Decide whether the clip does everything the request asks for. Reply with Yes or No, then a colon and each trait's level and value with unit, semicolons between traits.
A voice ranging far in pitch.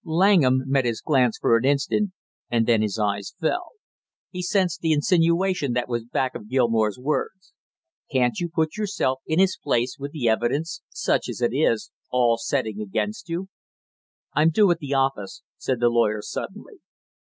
Yes: wide, 6.0 semitones